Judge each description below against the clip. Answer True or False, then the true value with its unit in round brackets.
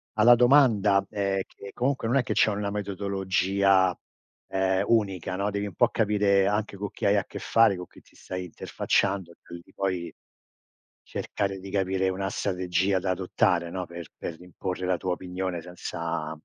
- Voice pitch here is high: False (95 Hz)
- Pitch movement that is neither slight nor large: False (1.8 semitones)